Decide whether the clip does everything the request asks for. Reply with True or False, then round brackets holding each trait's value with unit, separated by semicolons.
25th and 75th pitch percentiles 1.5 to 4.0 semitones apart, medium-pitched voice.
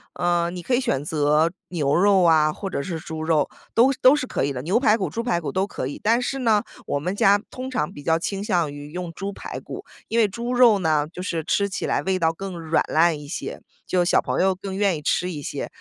False (4.5 semitones; 180 Hz)